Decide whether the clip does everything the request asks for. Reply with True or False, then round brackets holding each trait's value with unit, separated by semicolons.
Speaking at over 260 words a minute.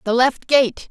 False (200 wpm)